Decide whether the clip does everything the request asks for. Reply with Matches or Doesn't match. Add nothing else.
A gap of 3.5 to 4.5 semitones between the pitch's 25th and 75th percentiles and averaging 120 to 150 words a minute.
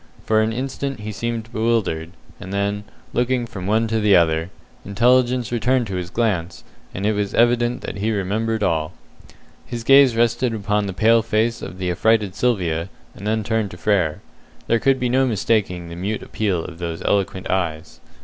Doesn't match